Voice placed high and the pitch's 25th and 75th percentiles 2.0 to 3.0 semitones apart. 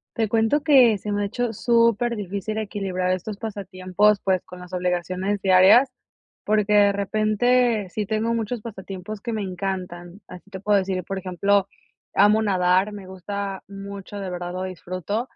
Yes: high, 200 Hz; narrow, 2.6 semitones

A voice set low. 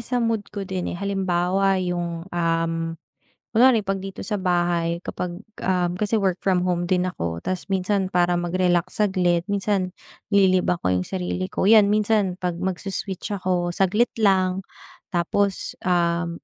No: medium, 185 Hz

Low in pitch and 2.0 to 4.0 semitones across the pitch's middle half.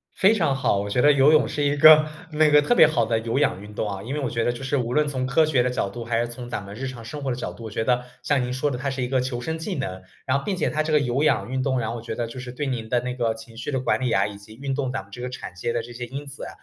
Yes: low, 125 Hz; average, 3.5 semitones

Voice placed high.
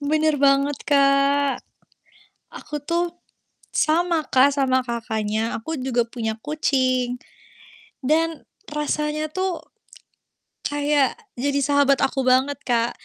Yes: very high, 280 Hz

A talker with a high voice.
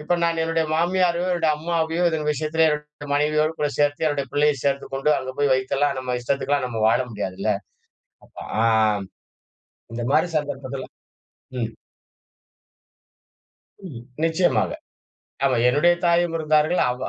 No: medium, 150 Hz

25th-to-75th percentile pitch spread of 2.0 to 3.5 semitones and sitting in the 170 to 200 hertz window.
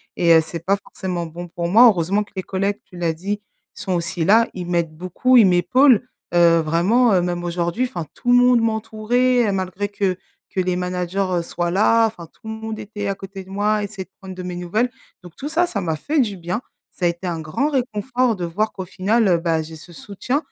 No: average, 4.1 semitones; high, 190 Hz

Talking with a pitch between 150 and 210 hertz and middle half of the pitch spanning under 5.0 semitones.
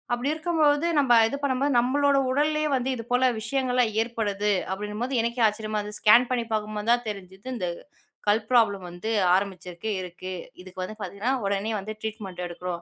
No: high, 220 Hz; average, 4.2 semitones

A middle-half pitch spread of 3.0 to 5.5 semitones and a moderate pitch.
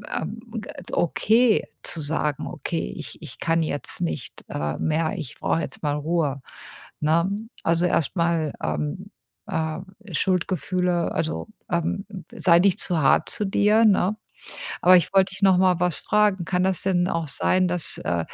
Yes: average, 3.3 semitones; medium, 170 Hz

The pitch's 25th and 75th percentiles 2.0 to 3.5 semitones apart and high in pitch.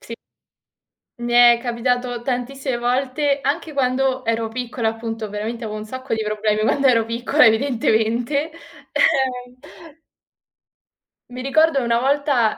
Yes: average, 2.8 semitones; high, 245 Hz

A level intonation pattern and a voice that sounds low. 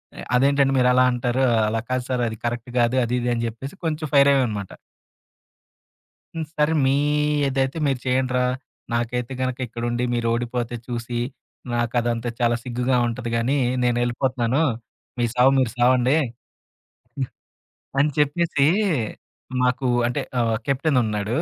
Yes: narrow, 2.0 semitones; low, 125 Hz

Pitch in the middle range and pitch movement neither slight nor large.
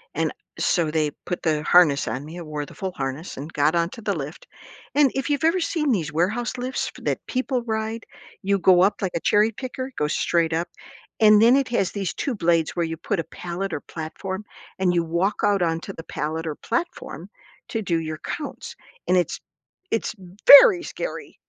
No: medium, 180 Hz; wide, 5.8 semitones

